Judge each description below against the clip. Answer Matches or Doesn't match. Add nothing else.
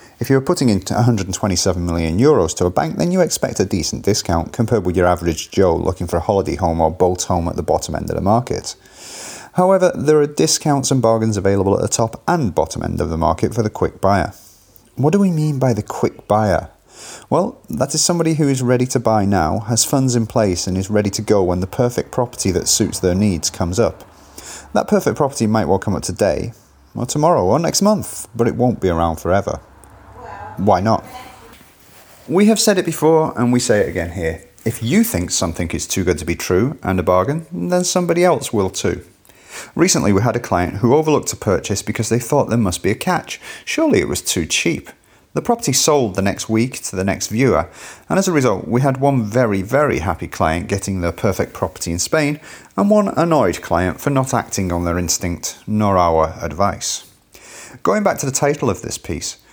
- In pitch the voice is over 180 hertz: Doesn't match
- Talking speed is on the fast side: Matches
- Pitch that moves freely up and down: Matches